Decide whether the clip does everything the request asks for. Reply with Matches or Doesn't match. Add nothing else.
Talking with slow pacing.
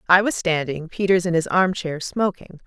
Doesn't match